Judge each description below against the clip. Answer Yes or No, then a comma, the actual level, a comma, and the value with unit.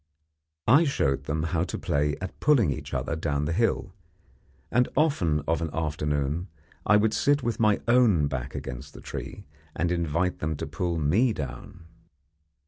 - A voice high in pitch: No, very low, 85 Hz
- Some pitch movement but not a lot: No, wide, 6.4 semitones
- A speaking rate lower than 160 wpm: No, average, 165 wpm